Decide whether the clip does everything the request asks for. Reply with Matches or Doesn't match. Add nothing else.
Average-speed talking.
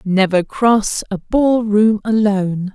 Doesn't match